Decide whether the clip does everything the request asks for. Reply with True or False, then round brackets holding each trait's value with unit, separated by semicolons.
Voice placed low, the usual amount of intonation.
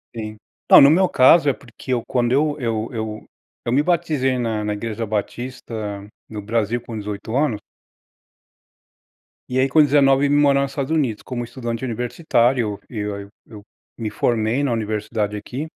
True (120 Hz; 4.1 semitones)